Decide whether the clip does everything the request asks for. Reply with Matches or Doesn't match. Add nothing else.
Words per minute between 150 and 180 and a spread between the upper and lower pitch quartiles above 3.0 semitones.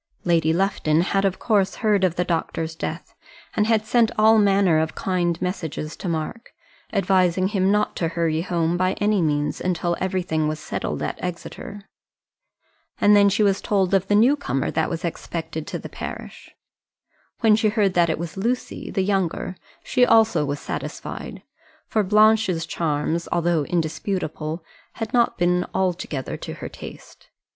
Matches